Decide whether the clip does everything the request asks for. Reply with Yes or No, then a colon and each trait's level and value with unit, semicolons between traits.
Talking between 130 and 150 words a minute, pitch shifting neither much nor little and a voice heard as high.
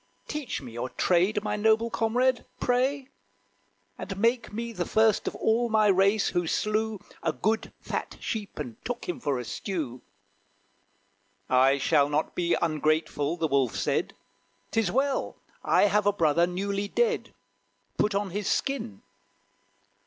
No: average, 145 wpm; wide, 6.0 semitones; high, 200 Hz